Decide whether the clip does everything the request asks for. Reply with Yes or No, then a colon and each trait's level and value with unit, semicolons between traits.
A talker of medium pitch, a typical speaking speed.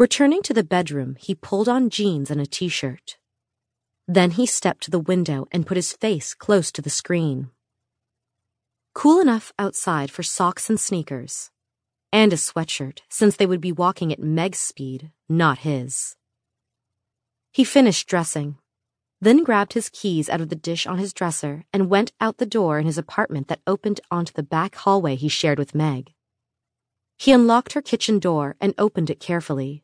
Yes: medium, 165 Hz; average, 175 wpm